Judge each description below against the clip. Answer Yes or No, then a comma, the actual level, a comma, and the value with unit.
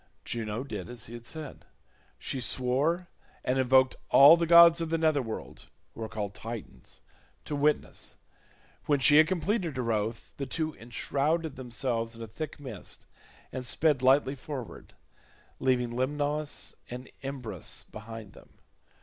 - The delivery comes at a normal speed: Yes, average, 150 wpm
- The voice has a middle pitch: No, low, 130 Hz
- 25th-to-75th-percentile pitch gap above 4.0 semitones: Yes, average, 4.6 semitones